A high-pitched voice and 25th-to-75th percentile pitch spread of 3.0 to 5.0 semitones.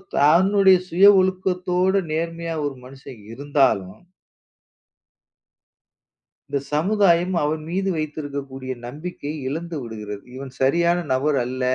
No: medium, 155 Hz; average, 4.7 semitones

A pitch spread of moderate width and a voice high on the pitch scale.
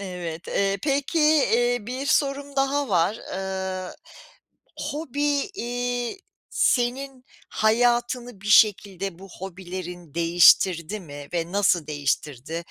No: wide, 5.8 semitones; high, 200 Hz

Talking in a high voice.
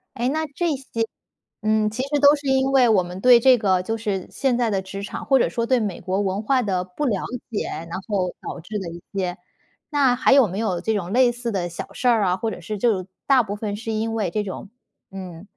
Yes: high, 215 Hz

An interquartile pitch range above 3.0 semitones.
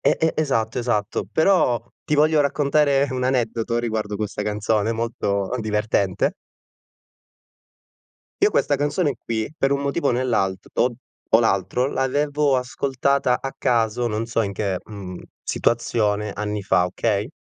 Yes: average, 4.4 semitones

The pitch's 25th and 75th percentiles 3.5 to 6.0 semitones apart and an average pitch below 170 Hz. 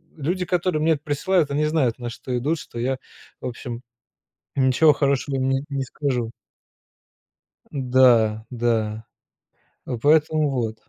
Yes: average, 4.0 semitones; low, 135 Hz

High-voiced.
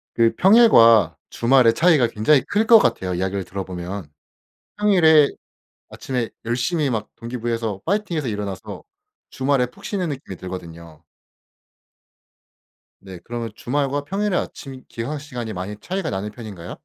No: low, 120 Hz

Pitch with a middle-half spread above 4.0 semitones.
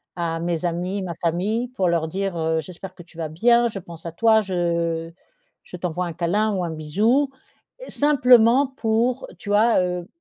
Yes: average, 4.8 semitones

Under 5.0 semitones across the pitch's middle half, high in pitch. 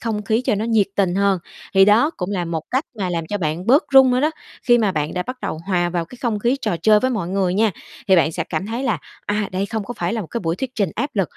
Yes: average, 4.5 semitones; high, 205 Hz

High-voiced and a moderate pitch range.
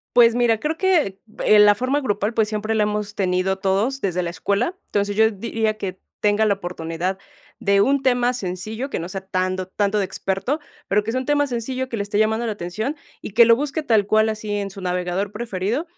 Yes: high, 210 Hz; average, 3.7 semitones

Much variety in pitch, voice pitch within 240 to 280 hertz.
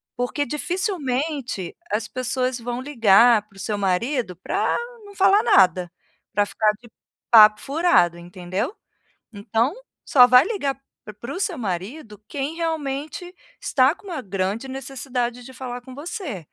Yes: wide, 5.7 semitones; very high, 250 Hz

